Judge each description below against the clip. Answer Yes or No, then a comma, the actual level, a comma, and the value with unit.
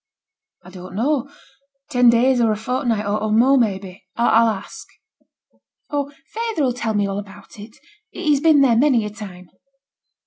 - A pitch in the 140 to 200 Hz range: No, high, 230 Hz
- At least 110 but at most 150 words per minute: No, average, 160 wpm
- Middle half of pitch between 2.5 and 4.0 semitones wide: No, average, 4.6 semitones